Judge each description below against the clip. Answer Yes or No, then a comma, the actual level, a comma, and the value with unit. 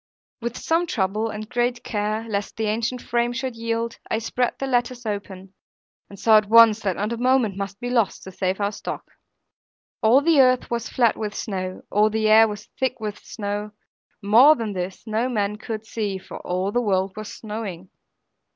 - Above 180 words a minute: Yes, average, 190 wpm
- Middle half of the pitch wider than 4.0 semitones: No, average, 2.8 semitones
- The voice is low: No, high, 220 Hz